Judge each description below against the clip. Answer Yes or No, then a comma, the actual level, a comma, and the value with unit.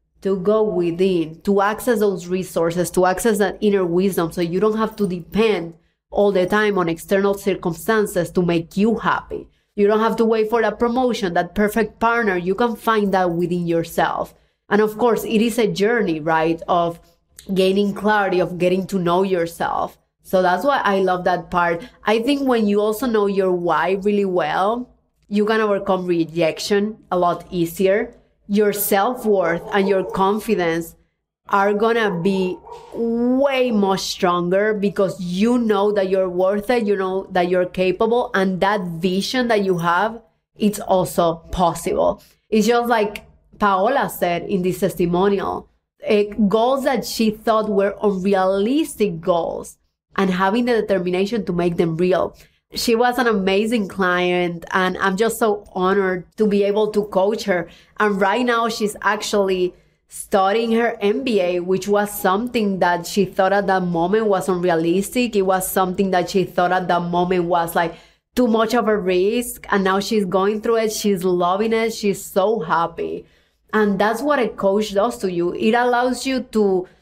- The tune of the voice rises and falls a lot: No, average, 3.0 semitones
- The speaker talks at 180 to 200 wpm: No, average, 170 wpm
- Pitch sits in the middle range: No, high, 200 Hz